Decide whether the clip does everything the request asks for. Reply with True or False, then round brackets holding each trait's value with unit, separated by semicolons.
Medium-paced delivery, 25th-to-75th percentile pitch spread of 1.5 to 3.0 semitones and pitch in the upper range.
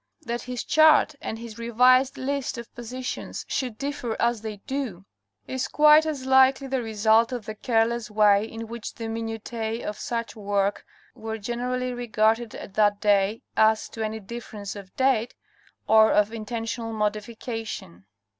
True (155 wpm; 2.6 semitones; 225 Hz)